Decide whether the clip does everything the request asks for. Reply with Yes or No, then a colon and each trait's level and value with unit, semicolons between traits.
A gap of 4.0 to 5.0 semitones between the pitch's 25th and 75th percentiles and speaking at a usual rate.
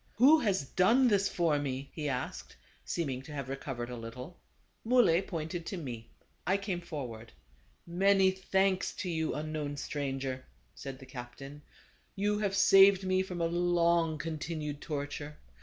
No: wide, 5.5 semitones; average, 160 wpm